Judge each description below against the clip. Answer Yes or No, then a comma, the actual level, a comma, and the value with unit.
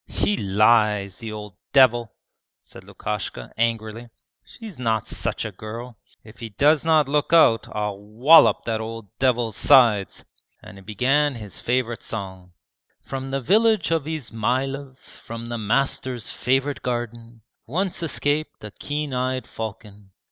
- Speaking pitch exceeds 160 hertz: No, low, 120 Hz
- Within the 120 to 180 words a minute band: Yes, average, 140 wpm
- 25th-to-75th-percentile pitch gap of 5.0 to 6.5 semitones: No, average, 4.2 semitones